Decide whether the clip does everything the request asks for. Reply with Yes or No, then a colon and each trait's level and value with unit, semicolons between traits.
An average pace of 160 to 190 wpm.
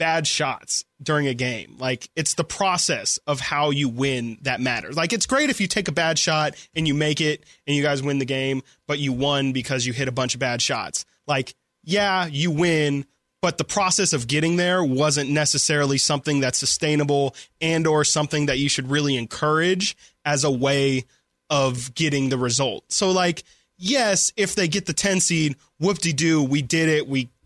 No: average, 200 wpm